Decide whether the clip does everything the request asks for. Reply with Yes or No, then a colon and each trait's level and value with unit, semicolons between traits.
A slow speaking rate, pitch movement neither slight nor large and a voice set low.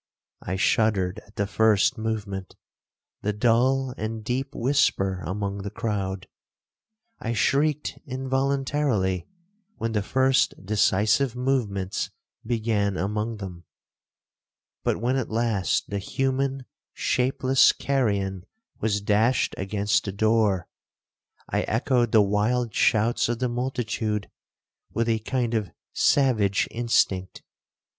Yes: slow, 110 wpm; average, 3.8 semitones; low, 110 Hz